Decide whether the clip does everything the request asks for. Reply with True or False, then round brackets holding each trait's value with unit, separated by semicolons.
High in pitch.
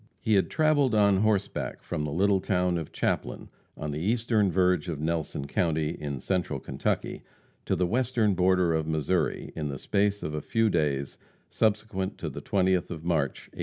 False (90 Hz)